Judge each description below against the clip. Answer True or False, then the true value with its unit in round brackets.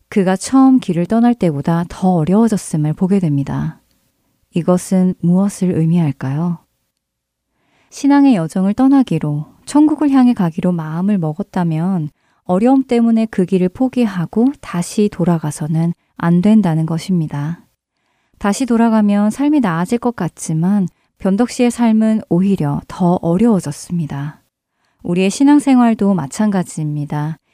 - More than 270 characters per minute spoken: True (290 characters per minute)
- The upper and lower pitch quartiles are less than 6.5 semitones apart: True (5.2 semitones)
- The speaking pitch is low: False (185 Hz)